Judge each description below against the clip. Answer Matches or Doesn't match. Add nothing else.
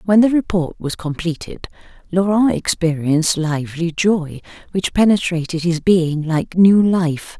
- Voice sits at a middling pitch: Matches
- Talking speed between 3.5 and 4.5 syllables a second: Matches